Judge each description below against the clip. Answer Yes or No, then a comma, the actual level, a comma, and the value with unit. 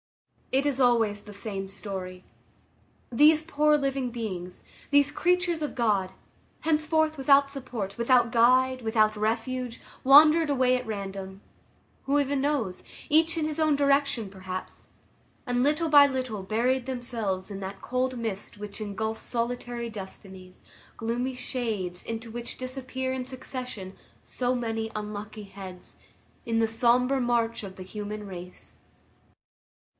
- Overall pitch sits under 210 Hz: No, high, 240 Hz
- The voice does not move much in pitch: No, average, 4.4 semitones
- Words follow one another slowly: Yes, slow, 130 wpm